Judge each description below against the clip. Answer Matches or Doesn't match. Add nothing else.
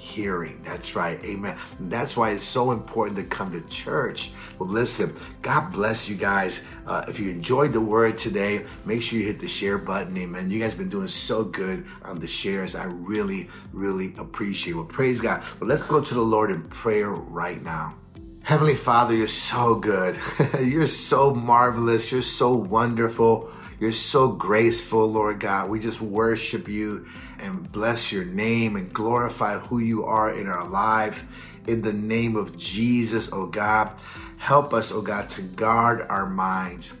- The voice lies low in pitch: Matches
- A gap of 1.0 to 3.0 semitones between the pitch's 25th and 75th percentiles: Matches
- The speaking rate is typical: Matches